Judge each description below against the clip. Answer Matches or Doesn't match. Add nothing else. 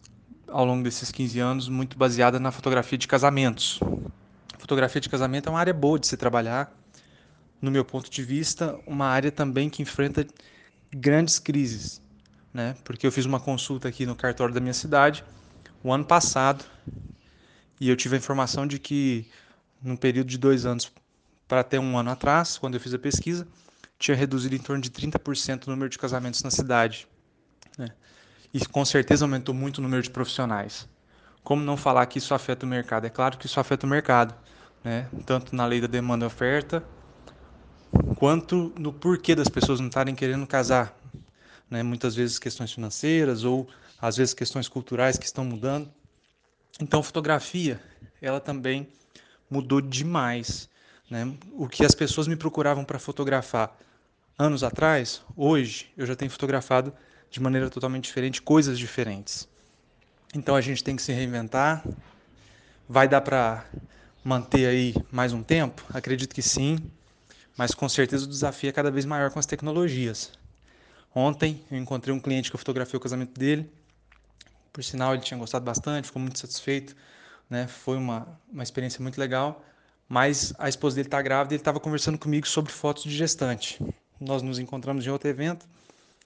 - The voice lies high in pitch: Doesn't match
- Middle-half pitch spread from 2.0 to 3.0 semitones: Matches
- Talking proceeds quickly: Doesn't match